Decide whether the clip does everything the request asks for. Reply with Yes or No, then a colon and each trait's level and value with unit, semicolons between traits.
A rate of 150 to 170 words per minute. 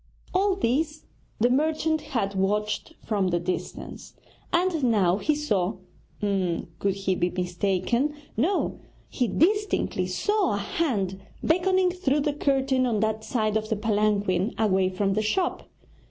No: average, 140 wpm